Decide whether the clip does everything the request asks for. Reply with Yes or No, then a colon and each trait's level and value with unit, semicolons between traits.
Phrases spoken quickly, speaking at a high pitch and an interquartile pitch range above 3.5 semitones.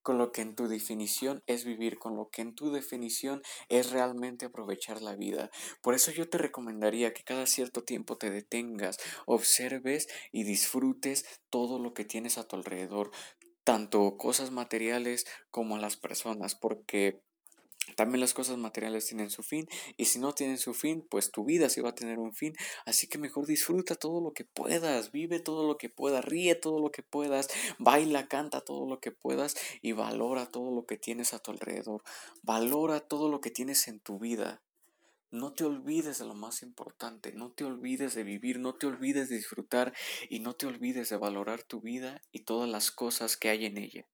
No: fast, 195 wpm; low, 125 Hz; average, 3.9 semitones